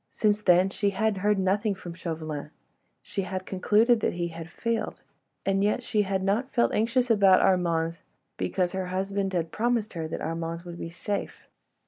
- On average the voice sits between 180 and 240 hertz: Yes, high, 190 Hz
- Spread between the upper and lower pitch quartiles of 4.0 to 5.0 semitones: No, average, 3.3 semitones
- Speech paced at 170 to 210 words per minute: Yes, average, 175 wpm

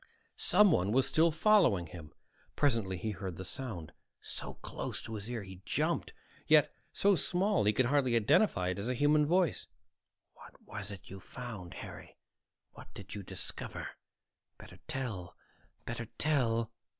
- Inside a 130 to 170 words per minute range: Yes, average, 150 wpm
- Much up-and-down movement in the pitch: Yes, wide, 7.3 semitones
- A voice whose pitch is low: Yes, low, 115 Hz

